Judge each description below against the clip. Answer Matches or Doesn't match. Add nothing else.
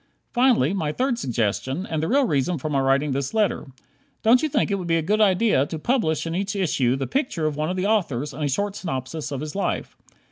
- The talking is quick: Matches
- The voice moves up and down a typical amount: Doesn't match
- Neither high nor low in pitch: Matches